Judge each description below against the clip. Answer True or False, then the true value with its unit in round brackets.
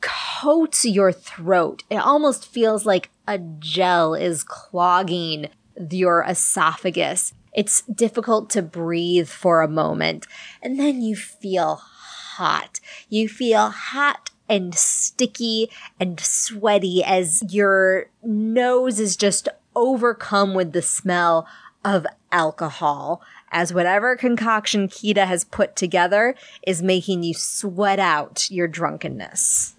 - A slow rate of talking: True (115 wpm)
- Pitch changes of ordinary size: True (4.2 semitones)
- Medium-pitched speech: False (195 Hz)